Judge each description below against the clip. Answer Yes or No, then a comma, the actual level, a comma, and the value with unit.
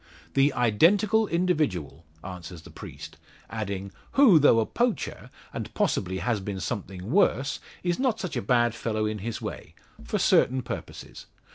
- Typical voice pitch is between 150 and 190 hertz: No, low, 120 Hz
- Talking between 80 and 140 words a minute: No, average, 150 wpm